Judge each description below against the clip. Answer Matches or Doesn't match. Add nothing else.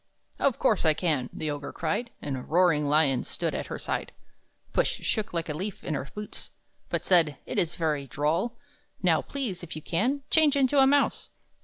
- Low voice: Doesn't match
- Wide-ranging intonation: Matches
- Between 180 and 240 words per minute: Matches